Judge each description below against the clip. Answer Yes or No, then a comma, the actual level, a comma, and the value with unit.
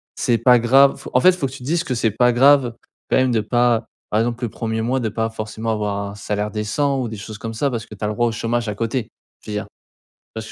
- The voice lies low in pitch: Yes, low, 115 Hz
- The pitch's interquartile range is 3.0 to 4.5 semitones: No, narrow, 2.5 semitones